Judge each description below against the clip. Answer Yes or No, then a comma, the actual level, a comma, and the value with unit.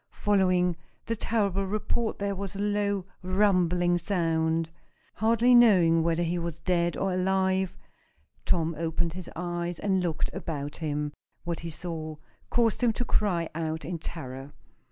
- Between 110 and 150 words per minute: Yes, average, 145 wpm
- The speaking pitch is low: No, medium, 175 Hz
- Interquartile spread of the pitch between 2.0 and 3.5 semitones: Yes, average, 3.2 semitones